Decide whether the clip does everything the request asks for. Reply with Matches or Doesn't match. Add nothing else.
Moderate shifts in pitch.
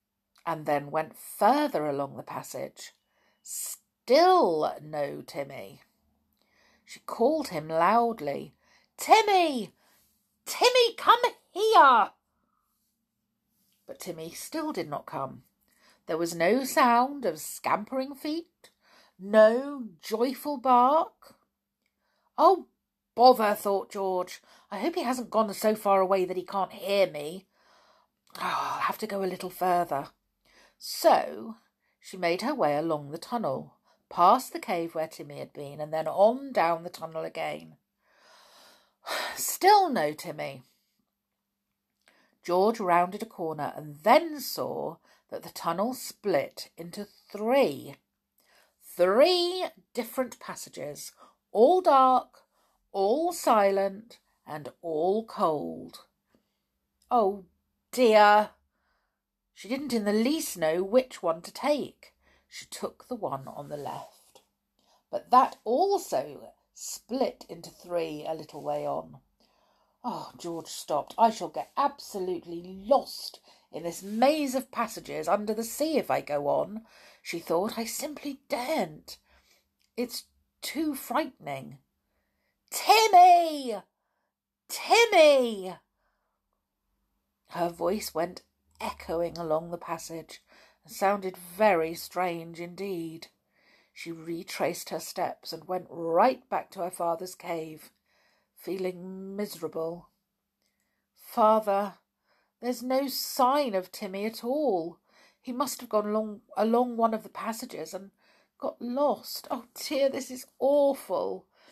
Doesn't match